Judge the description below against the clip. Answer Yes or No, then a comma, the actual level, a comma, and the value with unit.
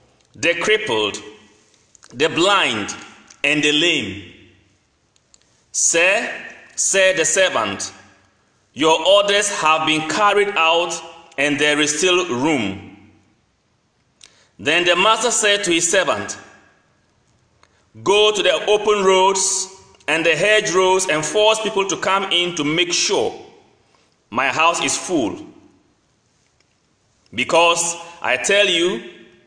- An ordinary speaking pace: No, slow, 110 wpm